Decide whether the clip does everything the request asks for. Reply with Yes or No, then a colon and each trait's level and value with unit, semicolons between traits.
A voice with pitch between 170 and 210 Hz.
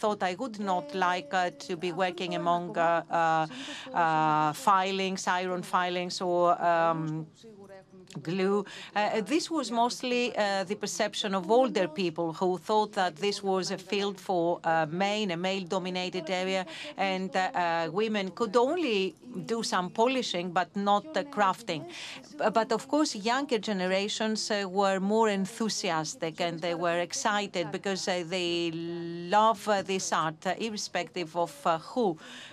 Yes: high, 190 Hz